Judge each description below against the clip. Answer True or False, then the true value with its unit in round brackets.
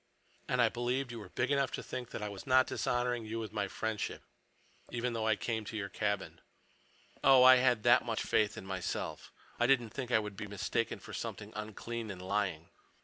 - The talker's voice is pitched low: True (115 Hz)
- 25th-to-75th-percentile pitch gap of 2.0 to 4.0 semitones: True (2.8 semitones)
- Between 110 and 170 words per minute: False (200 wpm)